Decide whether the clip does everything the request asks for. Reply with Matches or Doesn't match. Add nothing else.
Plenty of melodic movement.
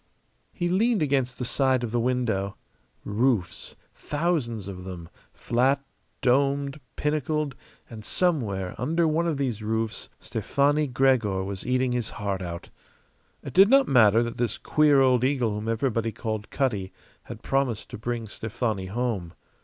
Doesn't match